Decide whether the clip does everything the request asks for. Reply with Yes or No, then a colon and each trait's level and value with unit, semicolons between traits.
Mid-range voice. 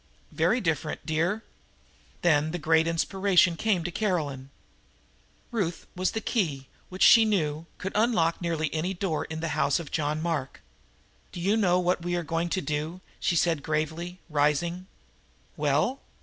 Yes: medium, 170 Hz